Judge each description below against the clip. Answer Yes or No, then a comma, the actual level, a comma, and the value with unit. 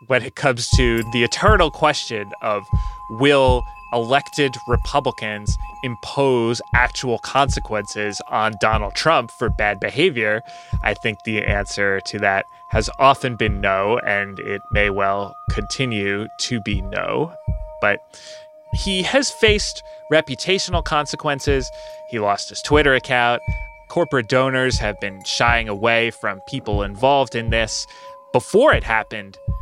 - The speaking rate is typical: No, slow, 130 wpm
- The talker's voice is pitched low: Yes, low, 120 Hz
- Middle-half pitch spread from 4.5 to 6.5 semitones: Yes, average, 5.3 semitones